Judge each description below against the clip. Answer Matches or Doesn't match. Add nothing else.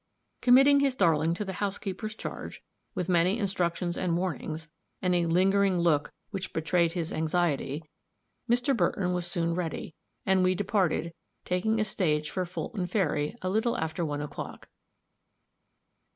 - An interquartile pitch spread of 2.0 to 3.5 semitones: Matches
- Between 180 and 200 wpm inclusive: Doesn't match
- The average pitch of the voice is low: Doesn't match